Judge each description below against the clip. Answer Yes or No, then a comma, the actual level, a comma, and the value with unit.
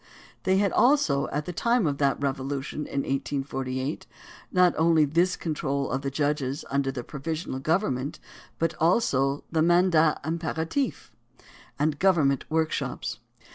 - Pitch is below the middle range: No, medium, 150 Hz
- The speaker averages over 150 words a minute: No, slow, 135 wpm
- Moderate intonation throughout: Yes, average, 3.5 semitones